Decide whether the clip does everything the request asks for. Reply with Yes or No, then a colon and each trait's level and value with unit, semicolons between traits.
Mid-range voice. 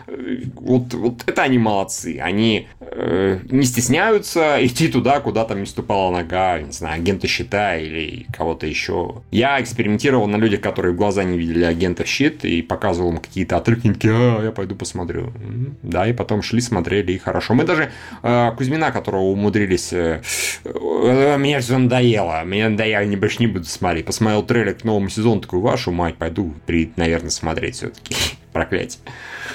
No: low, 105 Hz